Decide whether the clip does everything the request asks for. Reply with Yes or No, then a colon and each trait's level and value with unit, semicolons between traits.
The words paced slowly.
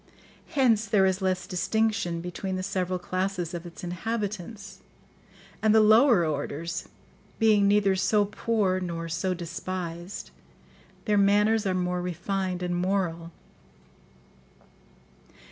Yes: slow, 115 wpm